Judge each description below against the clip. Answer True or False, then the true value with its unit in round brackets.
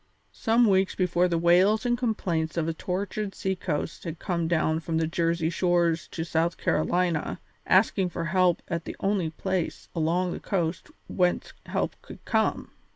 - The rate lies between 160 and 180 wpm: True (165 wpm)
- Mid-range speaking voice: True (175 Hz)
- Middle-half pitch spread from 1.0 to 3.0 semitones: True (2.4 semitones)